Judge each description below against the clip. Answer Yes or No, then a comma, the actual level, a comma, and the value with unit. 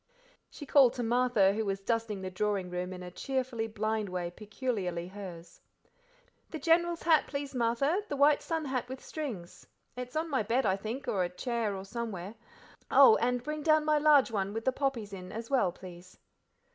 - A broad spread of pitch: Yes, wide, 5.8 semitones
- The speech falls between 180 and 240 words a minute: Yes, average, 190 wpm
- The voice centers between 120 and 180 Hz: No, high, 230 Hz